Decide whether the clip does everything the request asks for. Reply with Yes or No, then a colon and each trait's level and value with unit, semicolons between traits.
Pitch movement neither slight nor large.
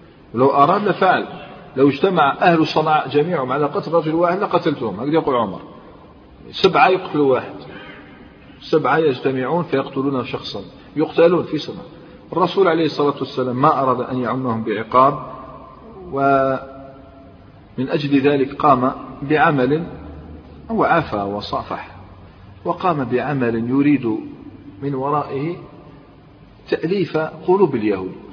Yes: average, 4.0 semitones